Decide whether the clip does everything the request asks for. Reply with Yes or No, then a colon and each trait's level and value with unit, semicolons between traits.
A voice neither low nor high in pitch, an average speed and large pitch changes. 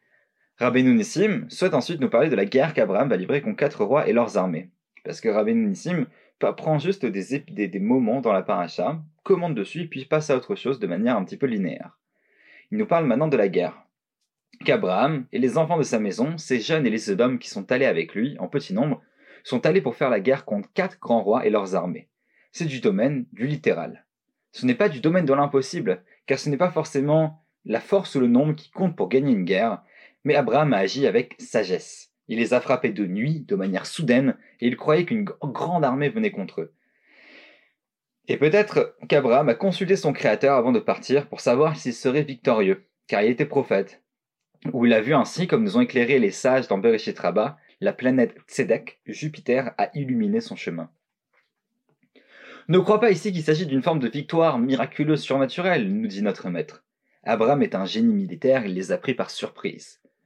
Yes: medium, 155 Hz; average, 205 wpm; wide, 7.1 semitones